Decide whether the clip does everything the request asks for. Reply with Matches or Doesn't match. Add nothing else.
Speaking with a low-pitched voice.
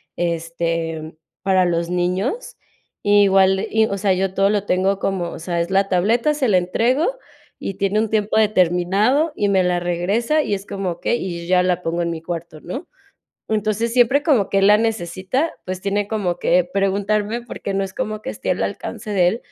Doesn't match